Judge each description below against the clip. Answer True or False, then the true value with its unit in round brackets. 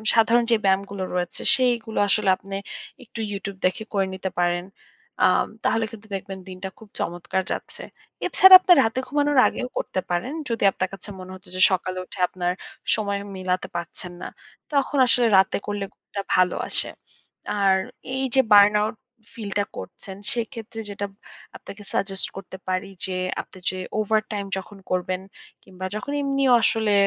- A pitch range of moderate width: True (3.1 semitones)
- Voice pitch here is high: True (200 Hz)